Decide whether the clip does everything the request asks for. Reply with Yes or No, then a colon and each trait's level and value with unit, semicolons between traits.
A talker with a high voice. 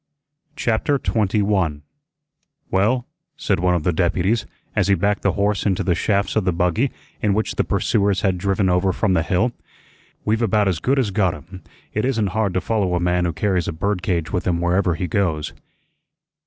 No: very low, 95 Hz